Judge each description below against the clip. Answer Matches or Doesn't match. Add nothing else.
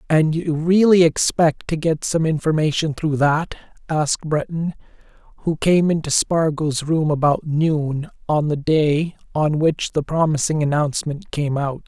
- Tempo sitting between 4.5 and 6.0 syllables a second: Doesn't match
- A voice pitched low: Doesn't match